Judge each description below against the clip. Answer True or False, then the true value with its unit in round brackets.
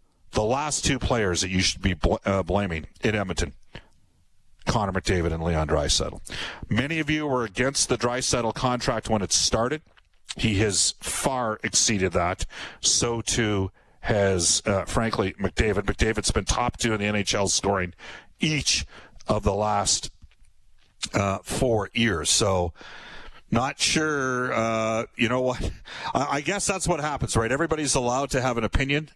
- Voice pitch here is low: True (110 Hz)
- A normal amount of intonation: True (4.8 semitones)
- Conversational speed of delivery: True (155 wpm)